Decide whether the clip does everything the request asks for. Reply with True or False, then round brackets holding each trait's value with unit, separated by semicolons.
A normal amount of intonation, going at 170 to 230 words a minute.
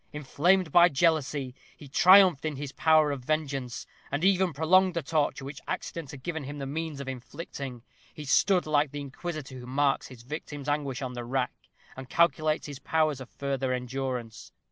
True (3.1 semitones; 180 wpm)